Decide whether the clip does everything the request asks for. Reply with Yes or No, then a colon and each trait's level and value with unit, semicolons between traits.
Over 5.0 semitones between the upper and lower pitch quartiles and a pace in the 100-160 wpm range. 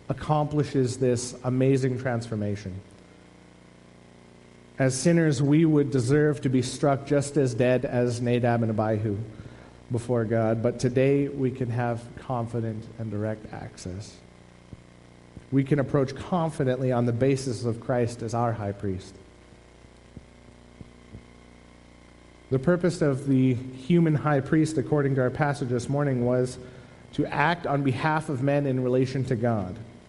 Yes: wide, 5.4 semitones; slow, 135 wpm